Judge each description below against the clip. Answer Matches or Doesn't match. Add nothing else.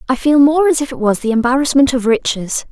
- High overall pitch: Matches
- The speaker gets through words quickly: Matches